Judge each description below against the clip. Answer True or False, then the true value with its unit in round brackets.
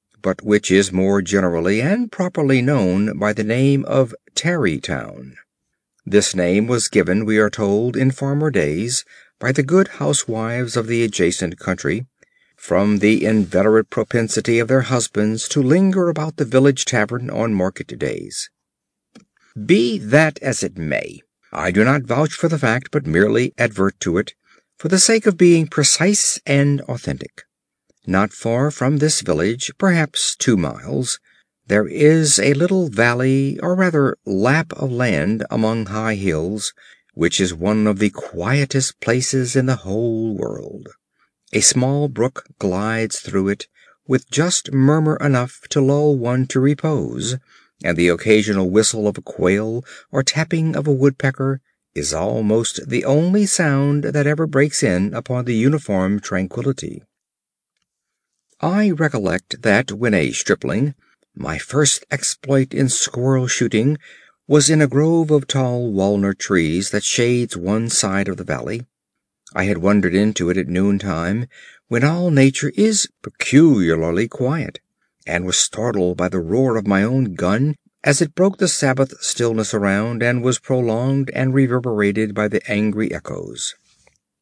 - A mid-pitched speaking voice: False (120 Hz)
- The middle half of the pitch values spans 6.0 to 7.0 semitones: False (5.3 semitones)